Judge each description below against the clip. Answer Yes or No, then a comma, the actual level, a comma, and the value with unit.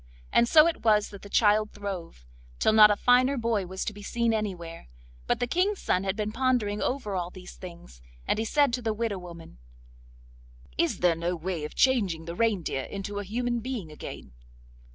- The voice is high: Yes, high, 205 Hz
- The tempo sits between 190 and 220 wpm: Yes, average, 195 wpm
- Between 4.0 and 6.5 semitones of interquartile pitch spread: Yes, average, 4.7 semitones